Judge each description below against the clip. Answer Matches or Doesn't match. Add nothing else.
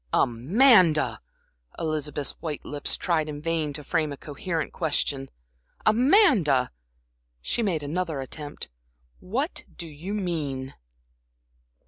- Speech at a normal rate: Doesn't match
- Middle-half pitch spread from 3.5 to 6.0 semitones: Matches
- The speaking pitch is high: Doesn't match